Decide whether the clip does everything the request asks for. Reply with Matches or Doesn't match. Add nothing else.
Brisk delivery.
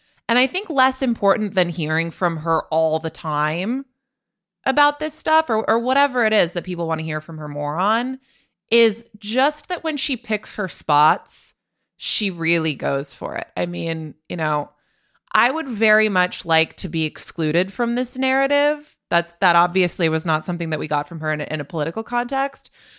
Doesn't match